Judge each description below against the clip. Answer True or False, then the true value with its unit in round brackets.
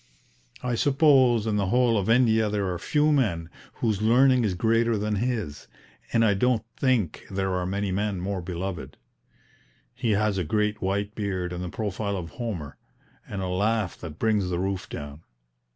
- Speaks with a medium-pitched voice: False (105 Hz)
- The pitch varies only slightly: False (3.6 semitones)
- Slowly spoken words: False (175 wpm)